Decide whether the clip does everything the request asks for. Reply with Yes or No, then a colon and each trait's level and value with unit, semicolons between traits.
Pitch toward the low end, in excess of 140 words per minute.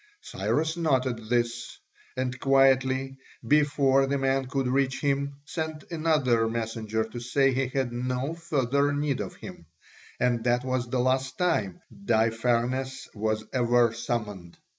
No: low, 130 Hz; slow, 135 wpm